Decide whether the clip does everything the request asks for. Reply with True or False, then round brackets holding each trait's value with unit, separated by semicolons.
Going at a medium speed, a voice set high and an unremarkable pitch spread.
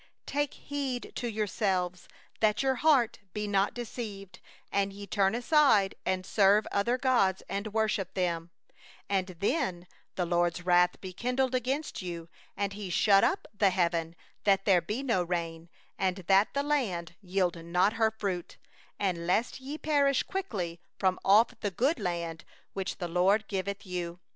True (160 wpm; 195 Hz; 4.8 semitones)